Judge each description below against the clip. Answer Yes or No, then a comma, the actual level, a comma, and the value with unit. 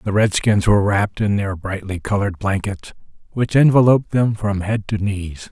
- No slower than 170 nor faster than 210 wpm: Yes, average, 175 wpm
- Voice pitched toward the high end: No, low, 100 Hz